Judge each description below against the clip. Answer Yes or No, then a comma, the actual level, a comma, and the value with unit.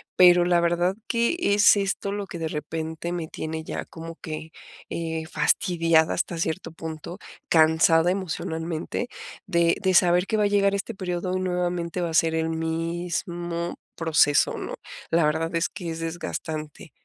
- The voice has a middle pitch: Yes, medium, 170 Hz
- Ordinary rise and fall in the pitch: No, narrow, 1.7 semitones